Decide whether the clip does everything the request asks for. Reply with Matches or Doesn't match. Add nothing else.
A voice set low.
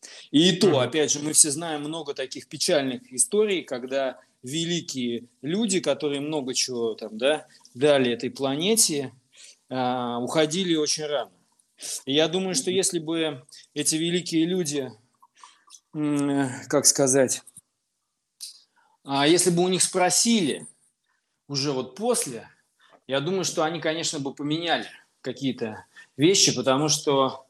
Doesn't match